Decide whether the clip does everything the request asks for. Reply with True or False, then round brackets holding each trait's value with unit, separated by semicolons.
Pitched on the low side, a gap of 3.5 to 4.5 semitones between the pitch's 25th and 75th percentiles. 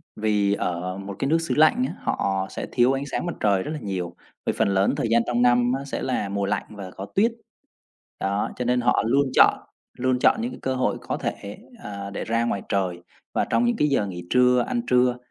False (115 Hz; 4.9 semitones)